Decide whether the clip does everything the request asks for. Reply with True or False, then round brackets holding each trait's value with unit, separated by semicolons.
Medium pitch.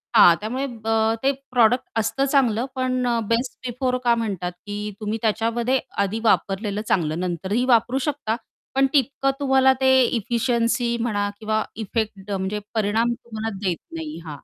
False (225 Hz)